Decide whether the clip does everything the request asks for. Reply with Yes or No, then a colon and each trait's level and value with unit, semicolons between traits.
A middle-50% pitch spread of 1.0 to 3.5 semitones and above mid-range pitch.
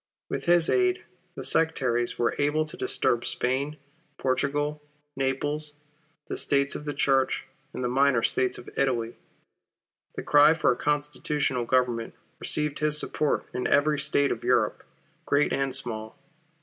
No: average, 2.9 semitones; medium, 140 Hz